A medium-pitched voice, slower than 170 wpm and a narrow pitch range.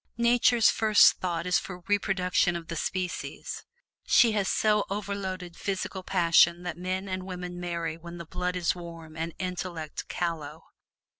Yes: medium, 180 Hz; average, 150 wpm; narrow, 2.2 semitones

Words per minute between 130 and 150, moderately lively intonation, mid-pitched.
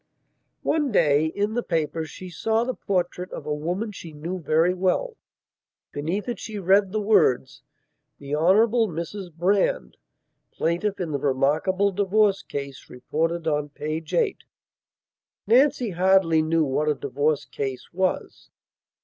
Yes: average, 140 wpm; average, 4.9 semitones; medium, 175 Hz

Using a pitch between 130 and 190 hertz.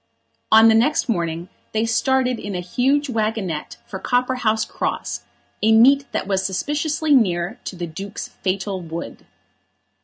No: high, 220 Hz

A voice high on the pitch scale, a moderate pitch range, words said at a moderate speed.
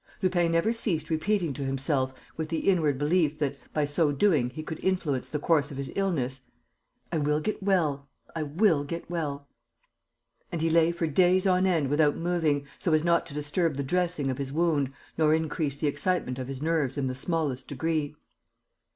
No: medium, 155 Hz; average, 3.2 semitones; average, 190 wpm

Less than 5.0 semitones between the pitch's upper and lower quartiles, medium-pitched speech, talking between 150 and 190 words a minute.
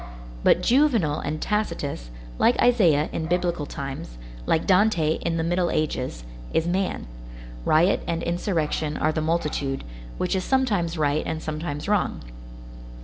No: average, 3.3 semitones; medium, 165 Hz; average, 140 wpm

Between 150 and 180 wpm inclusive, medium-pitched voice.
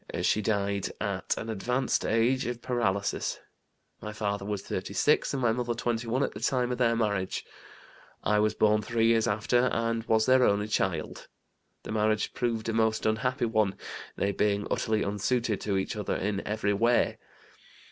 No: average, 165 wpm; low, 110 Hz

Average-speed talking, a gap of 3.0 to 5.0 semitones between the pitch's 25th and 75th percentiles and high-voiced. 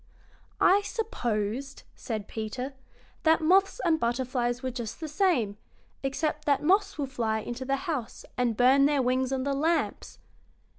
Yes: average, 150 wpm; average, 4.6 semitones; very high, 270 Hz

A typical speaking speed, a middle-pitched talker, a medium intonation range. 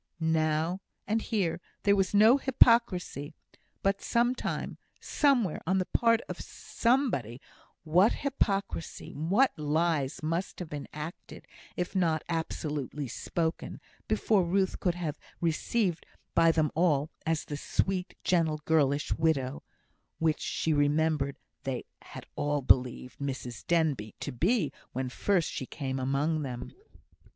No: slow, 130 wpm; medium, 160 Hz; average, 4.7 semitones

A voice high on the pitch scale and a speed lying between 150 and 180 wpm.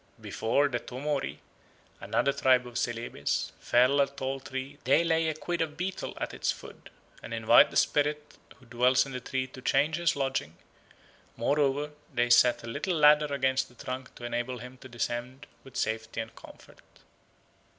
No: low, 130 Hz; average, 170 wpm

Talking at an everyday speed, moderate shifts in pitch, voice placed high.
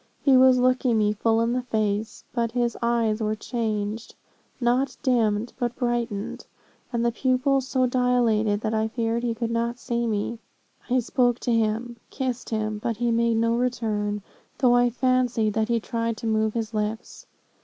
No: average, 175 wpm; narrow, 2.1 semitones; high, 235 Hz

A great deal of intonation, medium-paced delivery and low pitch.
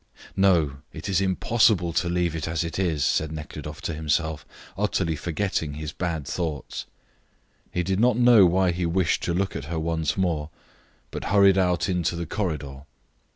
No: average, 3.3 semitones; average, 170 wpm; very low, 85 Hz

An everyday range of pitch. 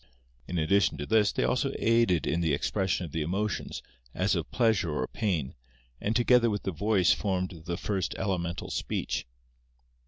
Yes: average, 4.3 semitones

